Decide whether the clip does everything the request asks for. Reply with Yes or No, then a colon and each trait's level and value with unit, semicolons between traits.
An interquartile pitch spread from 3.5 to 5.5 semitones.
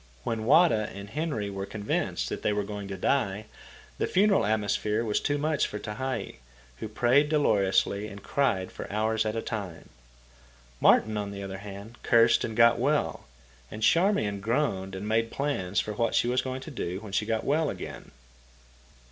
Yes: average, 4.1 semitones